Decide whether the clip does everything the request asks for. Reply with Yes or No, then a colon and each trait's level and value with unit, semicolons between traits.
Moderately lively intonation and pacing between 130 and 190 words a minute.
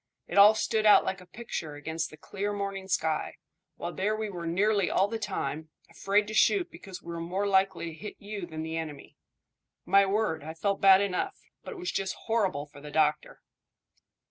No: average, 4.1 semitones; average, 200 wpm